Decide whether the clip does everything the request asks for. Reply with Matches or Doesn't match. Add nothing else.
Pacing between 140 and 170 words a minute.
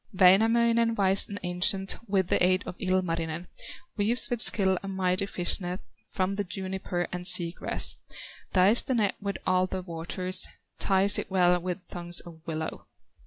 Matches